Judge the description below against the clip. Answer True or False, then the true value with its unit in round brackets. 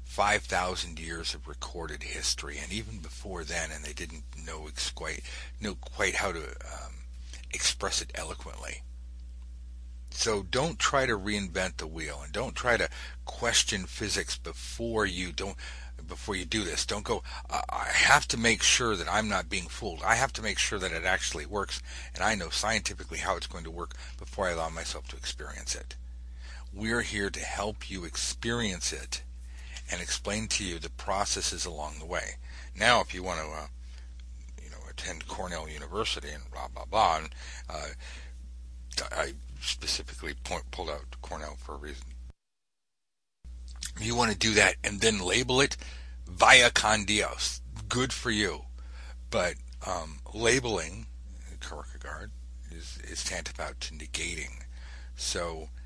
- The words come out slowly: False (160 wpm)